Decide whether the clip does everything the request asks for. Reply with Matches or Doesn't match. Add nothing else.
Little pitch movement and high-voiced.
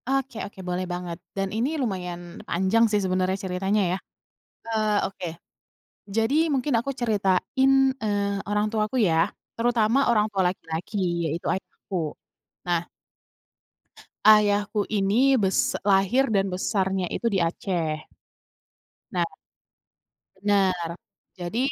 Doesn't match